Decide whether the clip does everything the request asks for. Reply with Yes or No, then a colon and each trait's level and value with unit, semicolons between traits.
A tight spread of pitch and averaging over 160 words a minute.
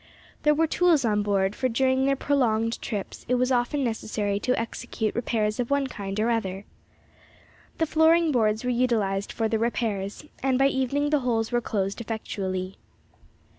No: average, 3.9 semitones; average, 170 wpm